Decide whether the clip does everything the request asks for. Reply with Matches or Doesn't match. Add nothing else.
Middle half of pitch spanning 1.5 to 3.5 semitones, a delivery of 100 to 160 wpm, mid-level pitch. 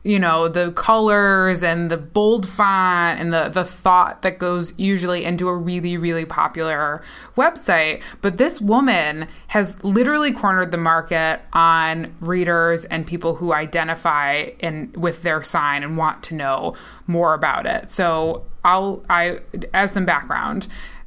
Matches